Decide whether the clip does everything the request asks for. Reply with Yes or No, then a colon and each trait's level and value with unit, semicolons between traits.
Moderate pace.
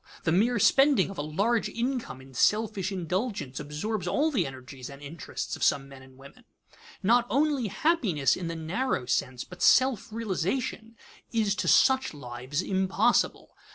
Yes: average, 155 wpm